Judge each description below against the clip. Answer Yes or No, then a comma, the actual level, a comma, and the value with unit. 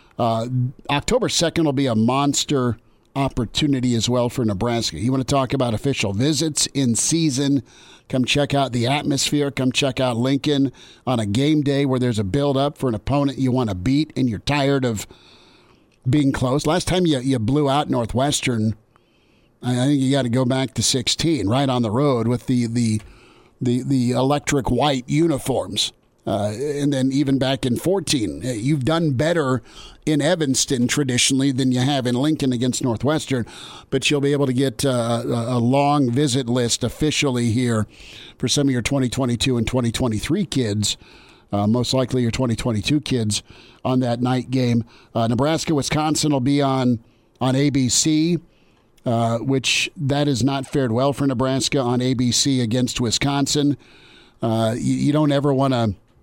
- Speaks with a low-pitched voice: Yes, low, 130 Hz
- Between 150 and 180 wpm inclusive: Yes, average, 170 wpm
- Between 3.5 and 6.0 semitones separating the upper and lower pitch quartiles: No, average, 2.8 semitones